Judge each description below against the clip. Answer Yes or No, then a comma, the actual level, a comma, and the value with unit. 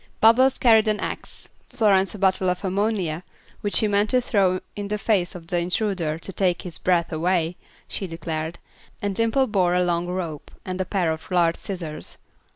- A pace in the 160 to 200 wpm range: Yes, average, 185 wpm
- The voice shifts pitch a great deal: No, average, 3.2 semitones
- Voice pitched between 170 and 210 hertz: Yes, medium, 185 Hz